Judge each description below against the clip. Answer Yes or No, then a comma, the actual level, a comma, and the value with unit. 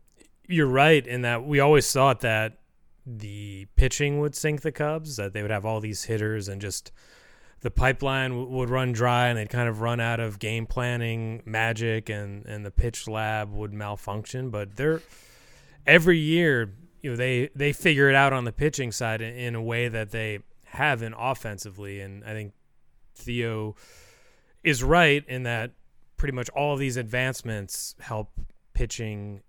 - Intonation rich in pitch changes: No, average, 3.9 semitones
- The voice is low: Yes, low, 120 Hz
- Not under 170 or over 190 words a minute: Yes, average, 175 wpm